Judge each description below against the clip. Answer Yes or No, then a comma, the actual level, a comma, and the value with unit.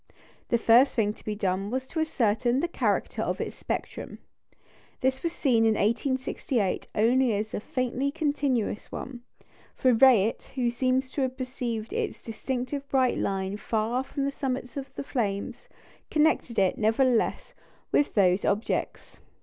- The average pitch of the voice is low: No, high, 245 Hz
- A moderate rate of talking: Yes, average, 150 wpm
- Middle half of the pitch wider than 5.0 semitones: No, average, 3.3 semitones